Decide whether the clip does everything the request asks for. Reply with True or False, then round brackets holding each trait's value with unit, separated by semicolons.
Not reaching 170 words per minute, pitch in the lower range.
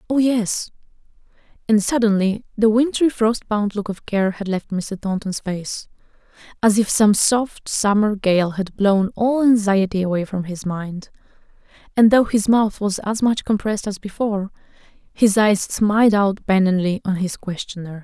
False (160 wpm; 205 Hz)